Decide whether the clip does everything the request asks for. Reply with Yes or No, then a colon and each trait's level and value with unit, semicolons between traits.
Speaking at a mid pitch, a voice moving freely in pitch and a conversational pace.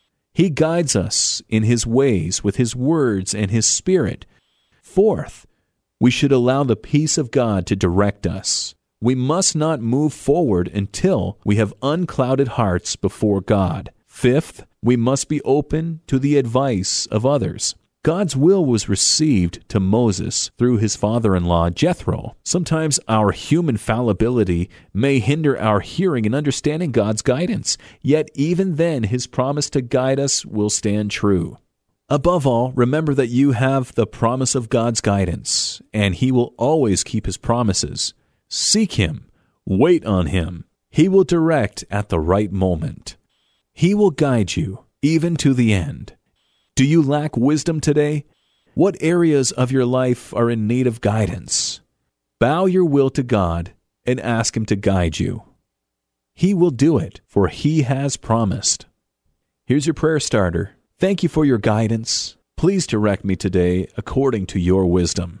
No: low, 120 Hz; wide, 6.2 semitones; average, 155 wpm